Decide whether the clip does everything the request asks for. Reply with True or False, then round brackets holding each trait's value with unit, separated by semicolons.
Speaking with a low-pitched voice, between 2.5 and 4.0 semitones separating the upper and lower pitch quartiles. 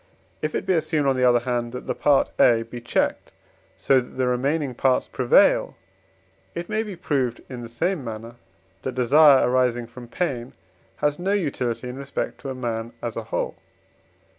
True (125 Hz; 3.5 semitones)